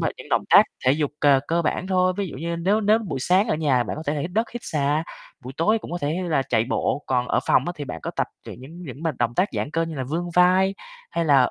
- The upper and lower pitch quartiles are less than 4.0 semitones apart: No, average, 4.7 semitones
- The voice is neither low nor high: Yes, medium, 160 Hz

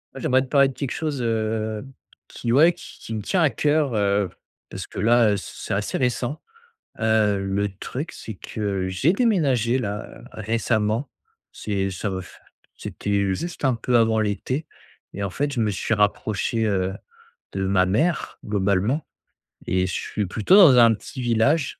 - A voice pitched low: Yes, low, 110 Hz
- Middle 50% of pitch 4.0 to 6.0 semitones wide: Yes, average, 4.5 semitones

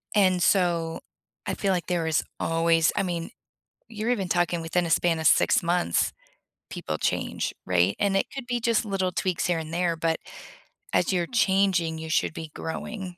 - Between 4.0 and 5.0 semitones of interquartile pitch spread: No, average, 2.9 semitones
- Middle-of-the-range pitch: Yes, medium, 175 Hz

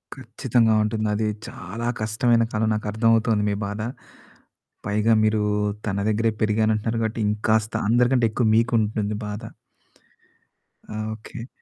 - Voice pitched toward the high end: No, low, 110 Hz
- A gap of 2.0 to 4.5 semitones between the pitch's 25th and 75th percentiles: No, narrow, 1.3 semitones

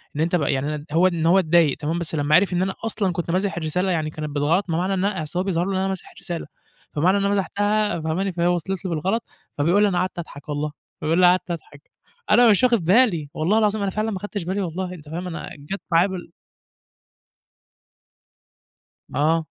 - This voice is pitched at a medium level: Yes, medium, 175 Hz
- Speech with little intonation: No, average, 3.4 semitones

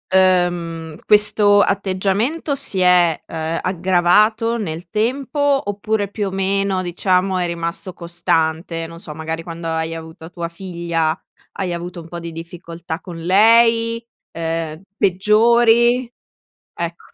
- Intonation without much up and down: No, average, 3.6 semitones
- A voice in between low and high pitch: Yes, medium, 180 Hz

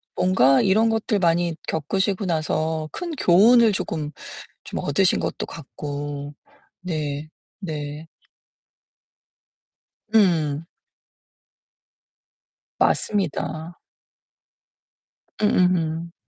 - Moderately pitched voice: Yes, medium, 165 Hz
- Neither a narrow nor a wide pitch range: Yes, average, 4.0 semitones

